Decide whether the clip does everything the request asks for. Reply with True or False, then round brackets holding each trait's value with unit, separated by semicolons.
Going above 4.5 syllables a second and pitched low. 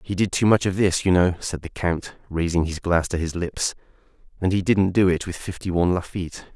True (5.5 syllables/s; 90 Hz)